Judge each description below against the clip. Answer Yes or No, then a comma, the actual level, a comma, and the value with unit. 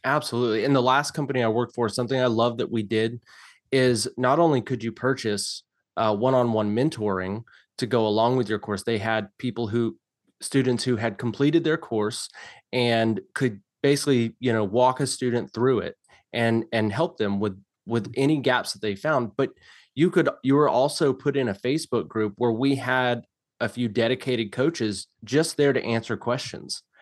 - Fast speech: No, average, 180 wpm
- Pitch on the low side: Yes, low, 120 Hz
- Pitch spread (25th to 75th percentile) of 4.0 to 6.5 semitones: No, average, 2.7 semitones